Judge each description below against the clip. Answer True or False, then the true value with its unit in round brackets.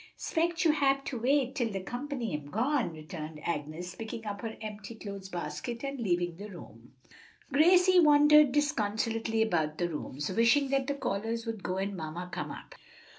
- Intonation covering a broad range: True (7.4 semitones)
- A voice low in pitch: False (225 Hz)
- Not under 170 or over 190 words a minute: True (175 wpm)